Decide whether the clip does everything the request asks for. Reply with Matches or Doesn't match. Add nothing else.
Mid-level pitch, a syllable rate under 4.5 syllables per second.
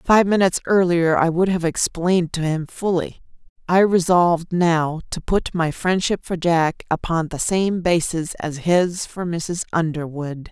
Matches